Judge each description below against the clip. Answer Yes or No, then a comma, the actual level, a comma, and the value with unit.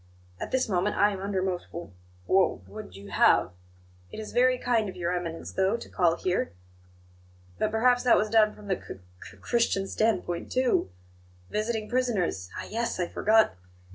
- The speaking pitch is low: No, high, 205 Hz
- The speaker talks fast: No, average, 175 wpm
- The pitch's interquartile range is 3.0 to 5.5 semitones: Yes, average, 4.3 semitones